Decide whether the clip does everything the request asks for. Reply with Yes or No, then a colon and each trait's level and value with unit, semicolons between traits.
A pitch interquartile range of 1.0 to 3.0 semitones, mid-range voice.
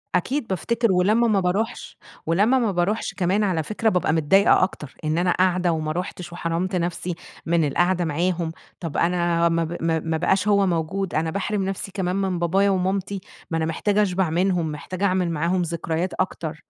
Yes: average, 2.7 semitones; medium, 180 Hz